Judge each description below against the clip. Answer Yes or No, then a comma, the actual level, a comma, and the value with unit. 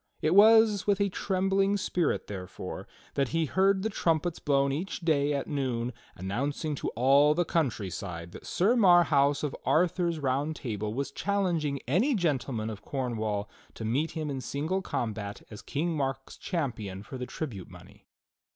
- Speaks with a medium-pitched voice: Yes, medium, 145 Hz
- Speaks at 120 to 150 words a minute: No, average, 160 wpm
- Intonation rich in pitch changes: Yes, wide, 6.2 semitones